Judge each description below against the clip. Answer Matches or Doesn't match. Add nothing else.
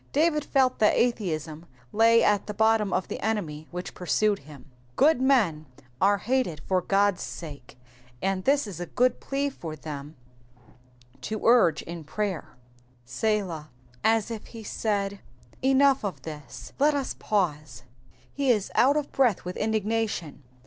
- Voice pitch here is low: Doesn't match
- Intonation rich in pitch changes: Matches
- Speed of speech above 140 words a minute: Matches